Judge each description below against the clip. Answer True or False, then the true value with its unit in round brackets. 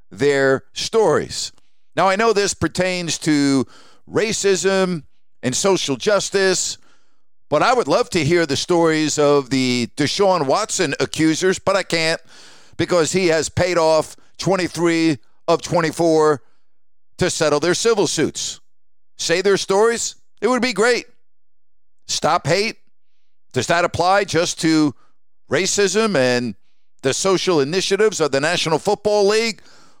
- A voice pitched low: False (170 Hz)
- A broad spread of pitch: False (4.9 semitones)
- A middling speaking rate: False (130 wpm)